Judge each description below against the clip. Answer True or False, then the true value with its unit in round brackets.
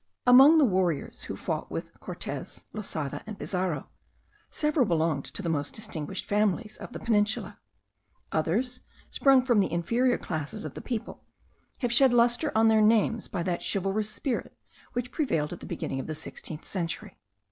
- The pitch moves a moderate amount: False (6.0 semitones)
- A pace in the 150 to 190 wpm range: True (165 wpm)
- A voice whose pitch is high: True (210 Hz)